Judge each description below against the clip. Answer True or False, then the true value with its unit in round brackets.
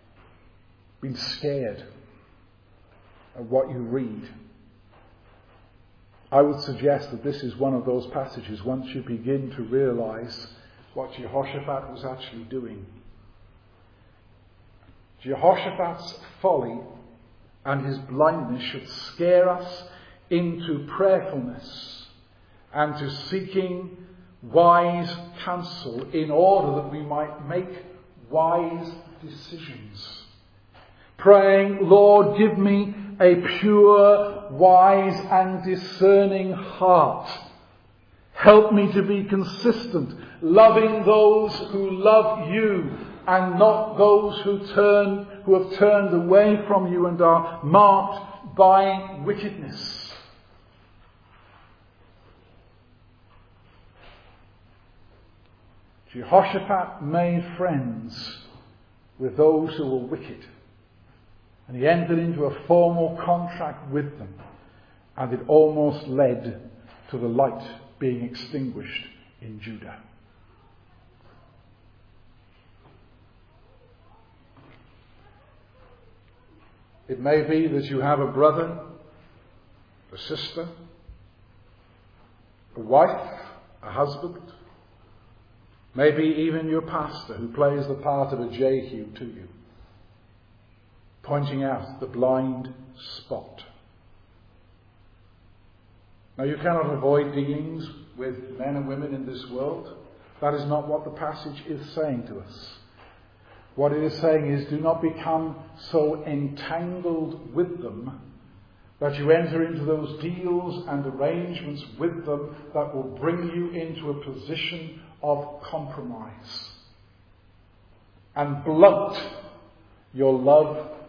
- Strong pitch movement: True (7.6 semitones)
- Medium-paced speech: False (100 wpm)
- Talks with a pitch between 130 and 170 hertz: True (135 Hz)